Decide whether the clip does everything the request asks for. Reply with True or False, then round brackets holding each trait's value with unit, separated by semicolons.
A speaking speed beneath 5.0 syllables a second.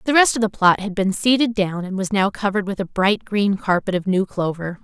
False (5.5 syllables/s)